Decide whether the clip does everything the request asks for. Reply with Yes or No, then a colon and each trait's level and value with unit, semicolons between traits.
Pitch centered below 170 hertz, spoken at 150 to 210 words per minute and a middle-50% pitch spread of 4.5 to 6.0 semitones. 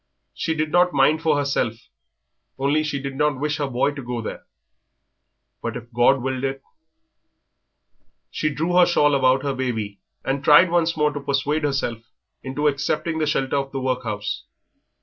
No: medium, 140 Hz; average, 170 wpm; narrow, 2.5 semitones